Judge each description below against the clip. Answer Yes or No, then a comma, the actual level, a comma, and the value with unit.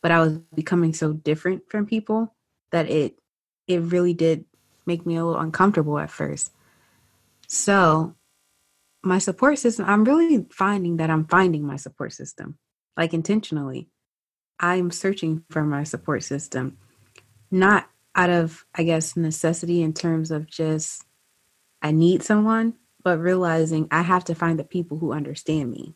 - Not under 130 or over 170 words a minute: Yes, average, 150 wpm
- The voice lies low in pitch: No, medium, 165 Hz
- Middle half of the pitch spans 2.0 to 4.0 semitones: Yes, average, 2.8 semitones